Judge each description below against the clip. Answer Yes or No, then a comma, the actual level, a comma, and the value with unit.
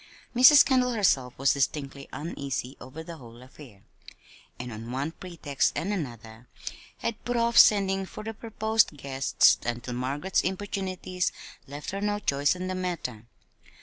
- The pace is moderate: Yes, average, 150 wpm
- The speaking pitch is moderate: Yes, medium, 160 Hz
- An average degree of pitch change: No, wide, 7.2 semitones